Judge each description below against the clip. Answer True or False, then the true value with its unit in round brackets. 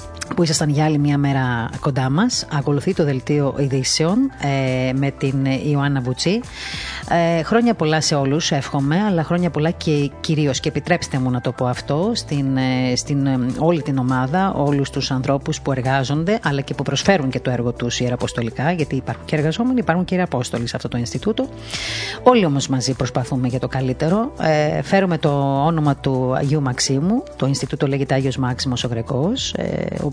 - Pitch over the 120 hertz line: True (140 Hz)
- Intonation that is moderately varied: True (3.8 semitones)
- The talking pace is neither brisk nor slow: False (175 wpm)